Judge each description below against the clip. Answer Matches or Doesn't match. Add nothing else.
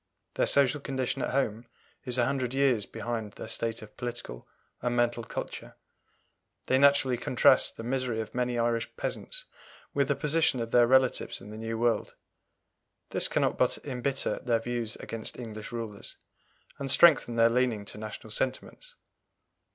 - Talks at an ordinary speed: Matches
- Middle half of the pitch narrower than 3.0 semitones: Matches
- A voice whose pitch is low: Matches